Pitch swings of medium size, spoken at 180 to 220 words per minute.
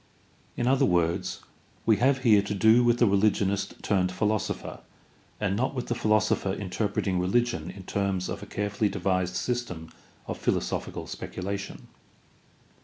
No: average, 3.5 semitones; average, 140 wpm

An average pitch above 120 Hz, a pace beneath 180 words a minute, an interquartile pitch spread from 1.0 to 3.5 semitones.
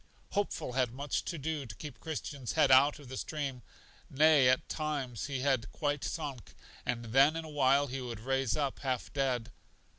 No: low, 135 Hz; average, 185 wpm; narrow, 2.6 semitones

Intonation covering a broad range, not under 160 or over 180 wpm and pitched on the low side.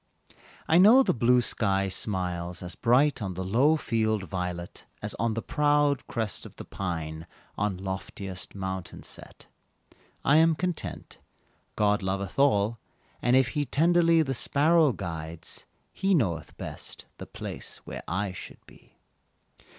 No: wide, 7.5 semitones; average, 145 wpm; low, 105 Hz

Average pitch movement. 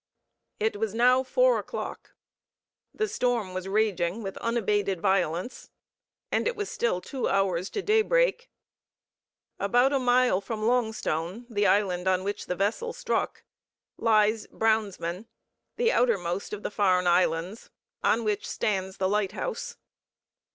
Yes: average, 4.6 semitones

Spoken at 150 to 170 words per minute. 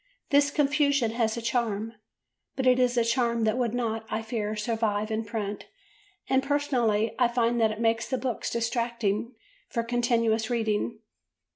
Yes: average, 160 wpm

